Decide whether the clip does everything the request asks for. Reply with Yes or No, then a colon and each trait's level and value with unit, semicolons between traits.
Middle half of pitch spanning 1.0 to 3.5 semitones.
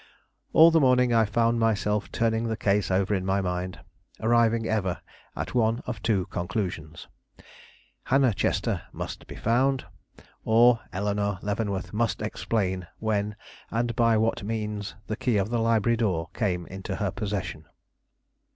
Yes: average, 2.9 semitones